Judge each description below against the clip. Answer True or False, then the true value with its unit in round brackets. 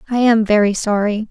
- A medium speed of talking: True (185 wpm)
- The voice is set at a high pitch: True (215 Hz)